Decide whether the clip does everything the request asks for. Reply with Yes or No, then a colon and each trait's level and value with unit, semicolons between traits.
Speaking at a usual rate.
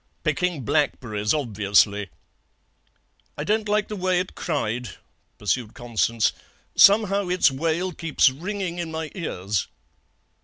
No: slow, 115 wpm